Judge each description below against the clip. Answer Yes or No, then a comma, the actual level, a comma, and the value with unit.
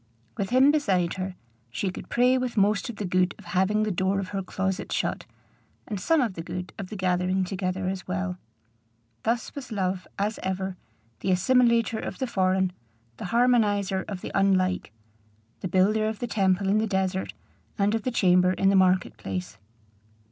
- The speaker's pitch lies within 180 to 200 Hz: Yes, high, 190 Hz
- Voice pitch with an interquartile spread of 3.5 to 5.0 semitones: No, average, 2.7 semitones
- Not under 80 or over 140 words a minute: No, average, 185 wpm